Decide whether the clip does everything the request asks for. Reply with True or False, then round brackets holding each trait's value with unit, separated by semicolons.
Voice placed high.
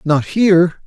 False (175 Hz)